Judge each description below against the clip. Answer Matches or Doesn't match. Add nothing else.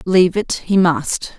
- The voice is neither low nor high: Matches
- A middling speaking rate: Matches